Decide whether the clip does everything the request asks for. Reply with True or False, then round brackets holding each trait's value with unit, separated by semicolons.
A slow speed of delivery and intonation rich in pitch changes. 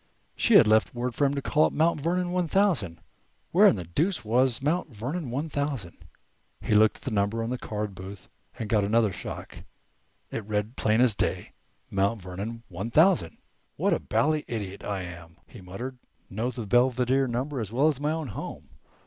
False (195 wpm; 5.8 semitones)